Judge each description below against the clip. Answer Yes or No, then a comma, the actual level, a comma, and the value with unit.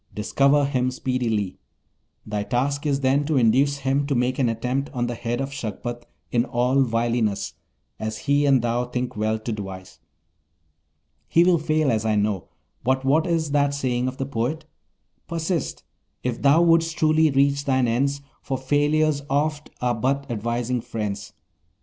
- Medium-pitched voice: No, low, 130 Hz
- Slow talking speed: No, average, 160 wpm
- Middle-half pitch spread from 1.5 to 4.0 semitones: Yes, average, 3.3 semitones